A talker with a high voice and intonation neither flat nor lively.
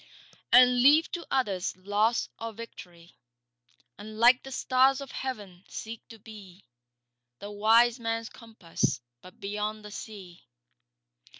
Yes: high, 220 Hz; average, 3.1 semitones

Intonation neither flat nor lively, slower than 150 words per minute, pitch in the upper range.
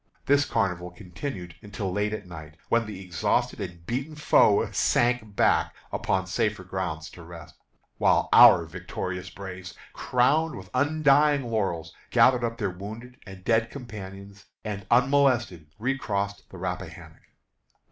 No: average, 5.0 semitones; slow, 135 wpm; low, 100 Hz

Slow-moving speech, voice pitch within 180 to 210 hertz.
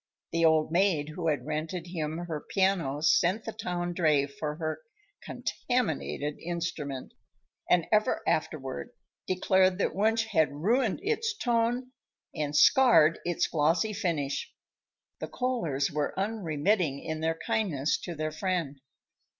No: slow, 130 wpm; medium, 170 Hz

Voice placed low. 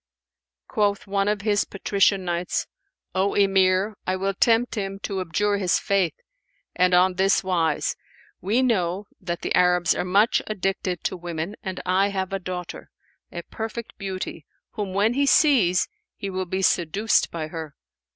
No: high, 190 Hz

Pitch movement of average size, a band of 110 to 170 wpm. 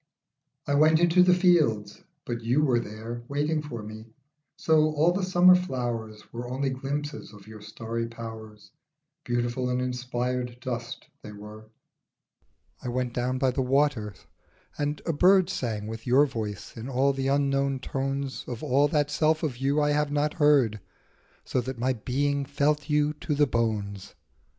Yes: average, 4.0 semitones; average, 165 wpm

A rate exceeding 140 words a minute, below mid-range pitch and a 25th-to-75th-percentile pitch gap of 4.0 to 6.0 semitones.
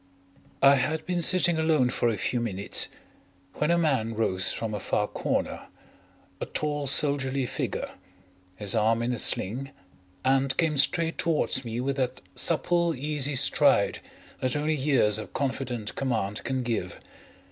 Yes: average, 150 wpm; low, 130 Hz; average, 4.6 semitones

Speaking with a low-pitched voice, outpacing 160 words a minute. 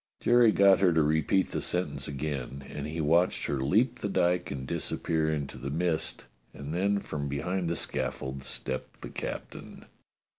Yes: very low, 80 Hz; average, 170 wpm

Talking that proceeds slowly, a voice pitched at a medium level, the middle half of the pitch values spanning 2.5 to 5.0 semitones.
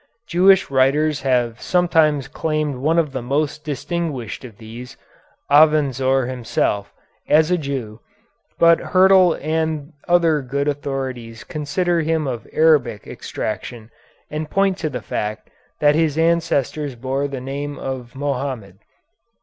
Yes: slow, 125 wpm; medium, 145 Hz; average, 3.6 semitones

